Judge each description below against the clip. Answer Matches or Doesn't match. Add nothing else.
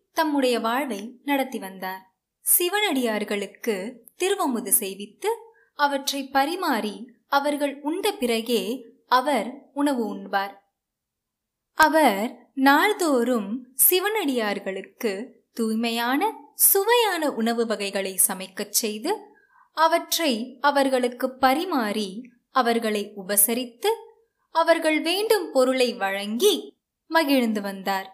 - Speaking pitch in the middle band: Doesn't match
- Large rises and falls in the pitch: Matches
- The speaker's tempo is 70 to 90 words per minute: Matches